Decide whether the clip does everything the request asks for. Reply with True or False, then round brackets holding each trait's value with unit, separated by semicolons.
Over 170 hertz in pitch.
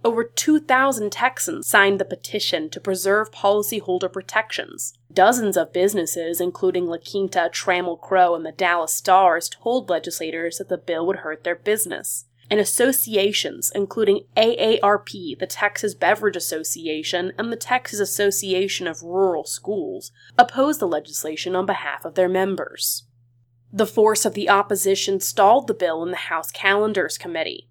True (190 Hz)